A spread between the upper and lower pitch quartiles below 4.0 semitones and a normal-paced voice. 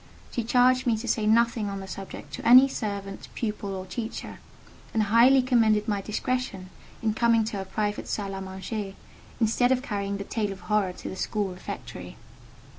Yes: average, 3.0 semitones; average, 185 wpm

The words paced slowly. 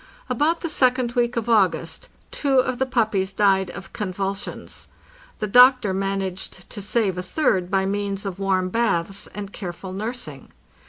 No: average, 155 wpm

